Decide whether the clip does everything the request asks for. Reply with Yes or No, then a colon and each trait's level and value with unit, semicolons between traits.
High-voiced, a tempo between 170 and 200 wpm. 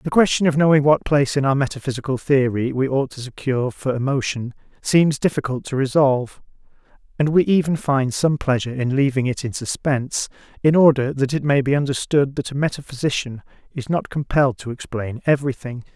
No: low, 135 Hz; average, 175 wpm